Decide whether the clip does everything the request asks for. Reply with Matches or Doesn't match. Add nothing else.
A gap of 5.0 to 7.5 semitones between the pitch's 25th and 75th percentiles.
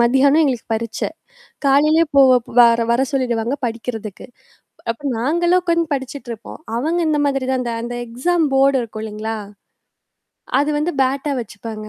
Doesn't match